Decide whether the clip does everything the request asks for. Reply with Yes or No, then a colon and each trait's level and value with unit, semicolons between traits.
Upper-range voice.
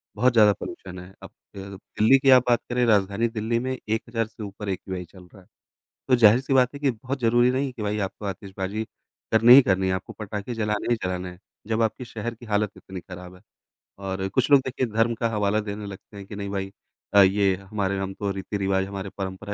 No: low, 105 Hz